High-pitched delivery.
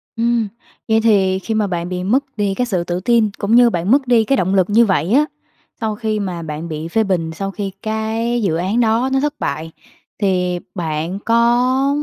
Yes: high, 205 Hz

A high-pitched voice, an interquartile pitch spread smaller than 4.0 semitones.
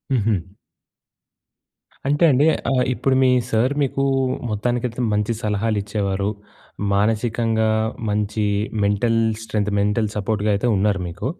No: low, 110 Hz; narrow, 2.6 semitones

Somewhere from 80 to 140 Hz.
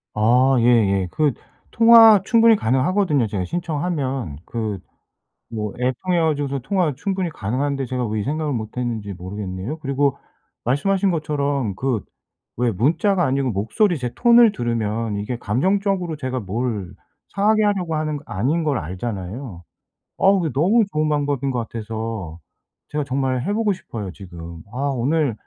Yes: low, 135 Hz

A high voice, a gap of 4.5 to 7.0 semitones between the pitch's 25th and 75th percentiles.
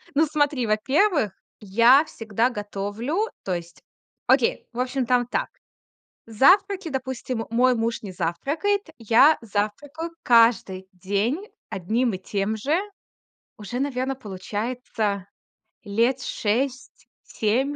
Yes: high, 235 Hz; average, 4.8 semitones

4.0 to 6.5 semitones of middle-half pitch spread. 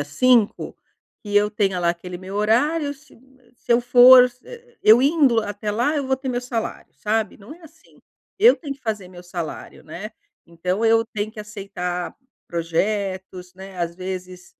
Yes: average, 5.3 semitones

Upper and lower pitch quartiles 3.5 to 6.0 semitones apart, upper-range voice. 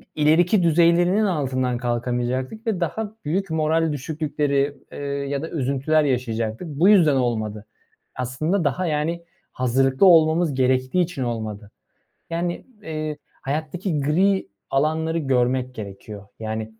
No: average, 4.7 semitones; medium, 145 Hz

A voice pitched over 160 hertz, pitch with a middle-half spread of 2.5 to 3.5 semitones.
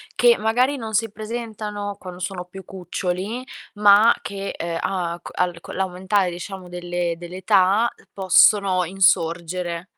Yes: high, 190 Hz; average, 2.8 semitones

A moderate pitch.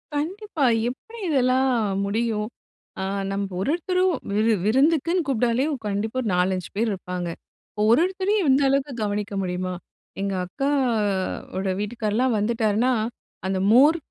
No: high, 235 Hz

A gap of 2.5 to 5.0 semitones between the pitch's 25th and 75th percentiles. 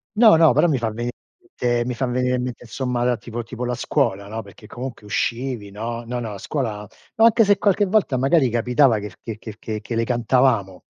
Yes: average, 2.9 semitones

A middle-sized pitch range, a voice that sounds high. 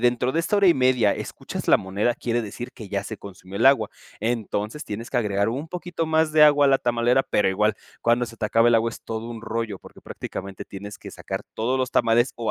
No: average, 3.5 semitones; low, 115 Hz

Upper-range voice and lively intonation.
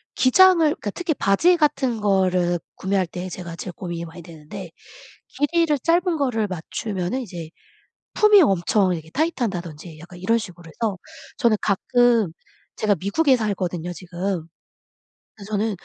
Yes: high, 200 Hz; wide, 6.3 semitones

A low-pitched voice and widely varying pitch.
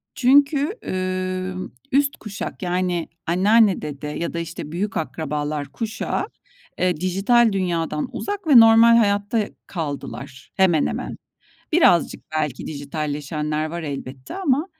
No: medium, 185 Hz; wide, 6.7 semitones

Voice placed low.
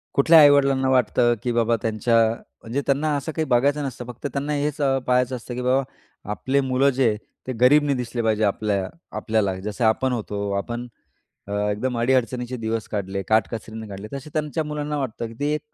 Yes: low, 125 Hz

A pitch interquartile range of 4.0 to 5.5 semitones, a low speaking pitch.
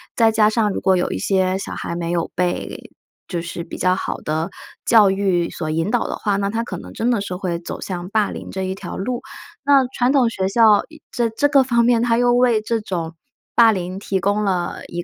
No: average, 4.3 semitones; high, 200 Hz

